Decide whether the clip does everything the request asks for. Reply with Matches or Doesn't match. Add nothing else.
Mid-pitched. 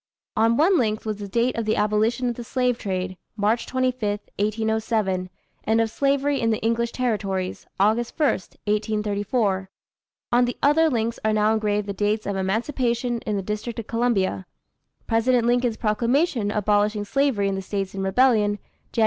Doesn't match